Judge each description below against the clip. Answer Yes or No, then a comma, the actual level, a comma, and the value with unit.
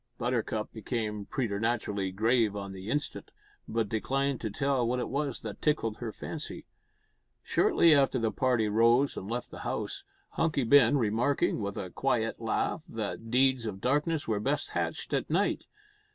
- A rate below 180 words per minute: Yes, average, 160 wpm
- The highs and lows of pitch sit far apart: No, average, 4.0 semitones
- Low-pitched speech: Yes, low, 115 Hz